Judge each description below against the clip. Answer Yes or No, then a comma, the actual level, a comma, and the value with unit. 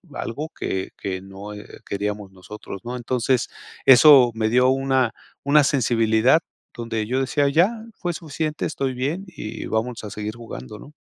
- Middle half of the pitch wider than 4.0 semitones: Yes, average, 4.6 semitones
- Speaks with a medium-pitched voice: No, low, 120 Hz